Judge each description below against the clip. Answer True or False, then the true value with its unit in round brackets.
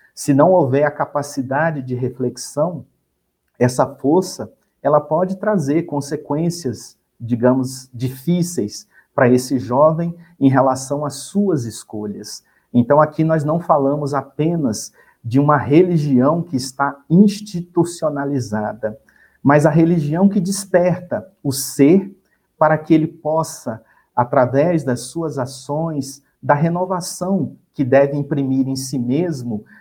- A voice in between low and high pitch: True (145 Hz)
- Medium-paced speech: False (115 wpm)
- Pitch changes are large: False (4.1 semitones)